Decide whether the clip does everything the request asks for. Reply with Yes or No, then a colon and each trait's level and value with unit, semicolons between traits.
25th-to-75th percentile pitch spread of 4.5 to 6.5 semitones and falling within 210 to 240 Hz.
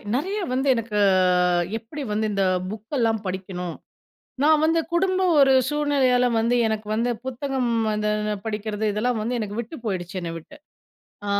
Yes: average, 4.8 semitones; high, 230 Hz